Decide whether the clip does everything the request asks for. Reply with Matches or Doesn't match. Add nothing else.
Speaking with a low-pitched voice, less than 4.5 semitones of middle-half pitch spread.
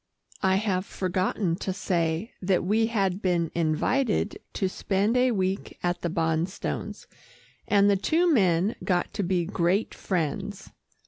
Doesn't match